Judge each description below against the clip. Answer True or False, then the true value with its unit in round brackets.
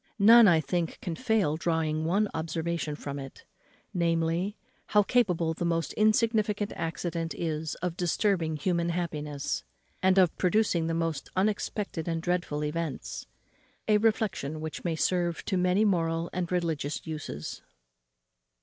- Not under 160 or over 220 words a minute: False (135 wpm)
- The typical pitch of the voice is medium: True (170 Hz)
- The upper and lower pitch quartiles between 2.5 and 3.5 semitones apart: True (2.8 semitones)